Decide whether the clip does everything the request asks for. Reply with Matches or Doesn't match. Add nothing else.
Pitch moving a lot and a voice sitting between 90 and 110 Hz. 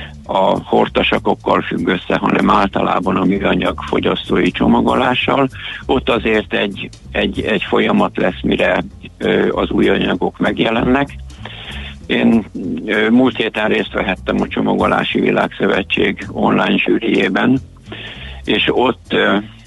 Matches